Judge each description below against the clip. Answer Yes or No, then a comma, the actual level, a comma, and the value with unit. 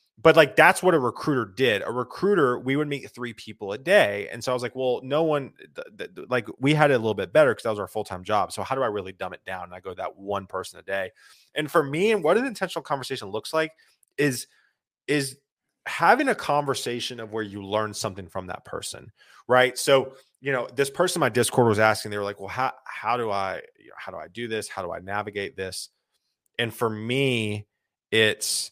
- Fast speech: Yes, fast, 240 wpm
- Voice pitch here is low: Yes, low, 125 Hz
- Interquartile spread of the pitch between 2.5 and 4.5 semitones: No, average, 5.0 semitones